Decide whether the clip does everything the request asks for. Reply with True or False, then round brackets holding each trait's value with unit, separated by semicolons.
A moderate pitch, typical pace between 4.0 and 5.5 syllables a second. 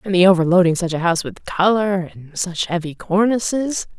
True (180 Hz; 5.3 syllables/s)